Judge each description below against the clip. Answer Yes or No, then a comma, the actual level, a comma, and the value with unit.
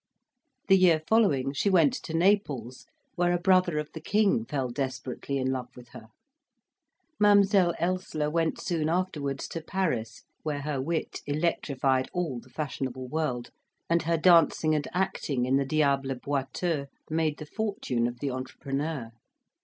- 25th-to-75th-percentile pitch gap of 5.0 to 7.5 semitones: No, average, 4.6 semitones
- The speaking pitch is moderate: Yes, medium, 150 Hz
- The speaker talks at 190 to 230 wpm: No, average, 150 wpm